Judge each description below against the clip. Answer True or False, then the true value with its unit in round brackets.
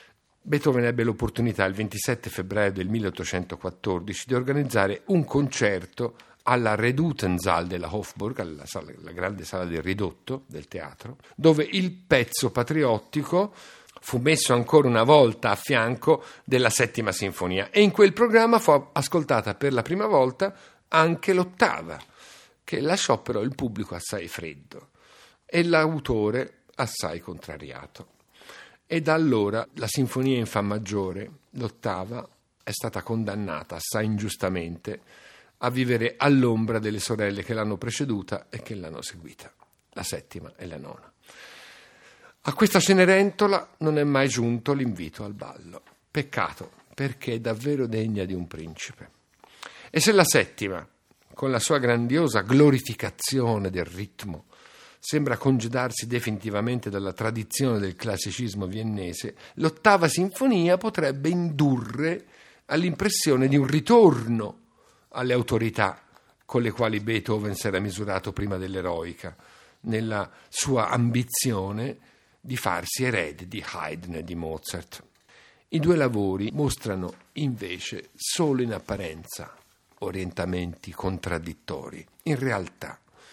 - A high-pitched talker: False (115 Hz)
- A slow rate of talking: False (125 wpm)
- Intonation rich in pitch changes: True (6.1 semitones)